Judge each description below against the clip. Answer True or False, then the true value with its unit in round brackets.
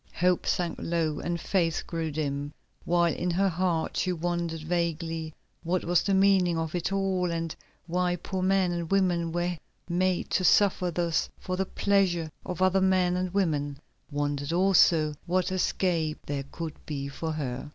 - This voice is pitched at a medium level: True (175 Hz)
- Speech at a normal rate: True (165 wpm)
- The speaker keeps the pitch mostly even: True (2.3 semitones)